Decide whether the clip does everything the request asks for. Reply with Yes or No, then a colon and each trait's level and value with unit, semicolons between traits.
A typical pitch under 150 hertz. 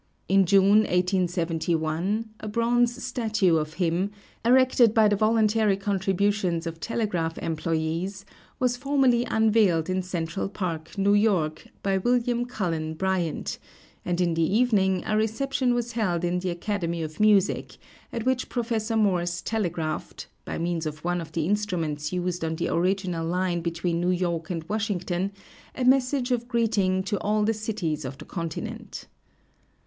No: high, 190 Hz